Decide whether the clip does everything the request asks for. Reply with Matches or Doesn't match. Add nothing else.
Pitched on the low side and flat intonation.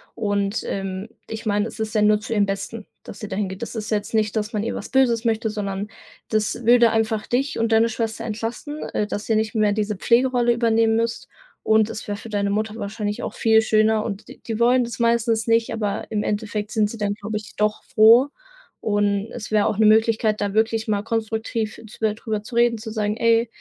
Doesn't match